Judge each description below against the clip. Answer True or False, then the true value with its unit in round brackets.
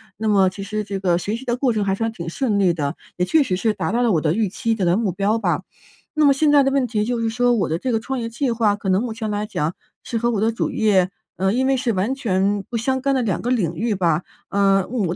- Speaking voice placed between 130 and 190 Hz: False (215 Hz)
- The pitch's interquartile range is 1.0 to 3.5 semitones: False (4.0 semitones)